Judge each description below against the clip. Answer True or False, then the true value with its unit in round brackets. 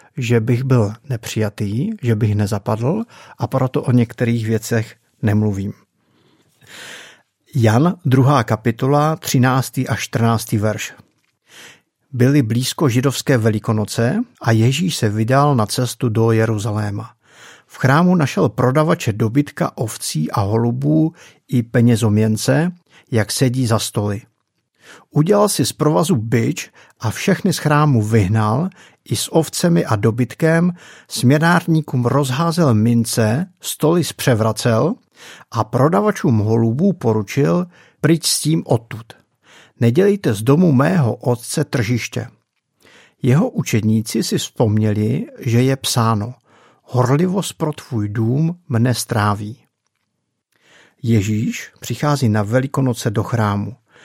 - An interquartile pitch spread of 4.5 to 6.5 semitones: True (4.9 semitones)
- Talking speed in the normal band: False (110 wpm)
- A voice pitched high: False (125 Hz)